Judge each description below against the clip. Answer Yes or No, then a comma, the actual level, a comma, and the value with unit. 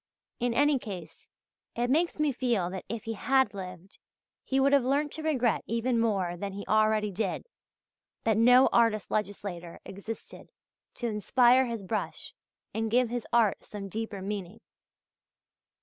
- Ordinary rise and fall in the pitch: Yes, average, 3.7 semitones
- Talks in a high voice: Yes, high, 225 Hz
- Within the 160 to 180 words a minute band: No, average, 150 wpm